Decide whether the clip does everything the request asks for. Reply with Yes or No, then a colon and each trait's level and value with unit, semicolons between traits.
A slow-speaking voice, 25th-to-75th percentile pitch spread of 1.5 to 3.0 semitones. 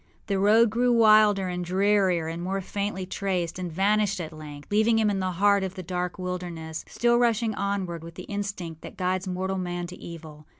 No: average, 200 wpm; narrow, 2.6 semitones